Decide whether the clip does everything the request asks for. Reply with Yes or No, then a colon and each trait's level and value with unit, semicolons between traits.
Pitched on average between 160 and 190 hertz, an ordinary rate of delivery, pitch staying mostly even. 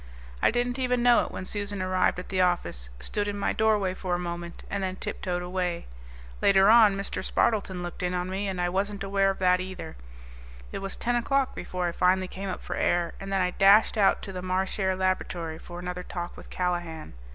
No: medium, 185 Hz; fast, 220 wpm; narrow, 1.9 semitones